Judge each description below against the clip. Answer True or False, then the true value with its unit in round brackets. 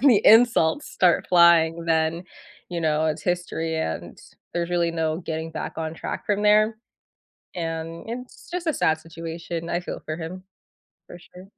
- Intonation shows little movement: True (2.3 semitones)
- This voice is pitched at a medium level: True (170 Hz)